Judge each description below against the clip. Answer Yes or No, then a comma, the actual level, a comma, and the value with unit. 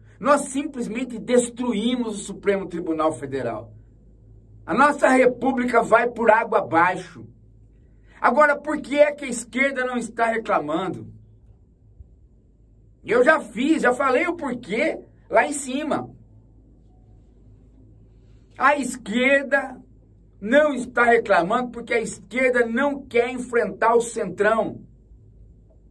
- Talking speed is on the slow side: Yes, slow, 110 wpm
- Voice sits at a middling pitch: No, high, 225 Hz